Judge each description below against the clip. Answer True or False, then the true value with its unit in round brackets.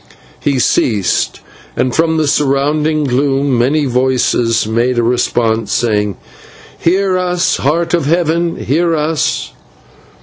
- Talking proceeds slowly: True (110 wpm)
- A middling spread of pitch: True (4.9 semitones)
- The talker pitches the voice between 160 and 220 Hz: False (140 Hz)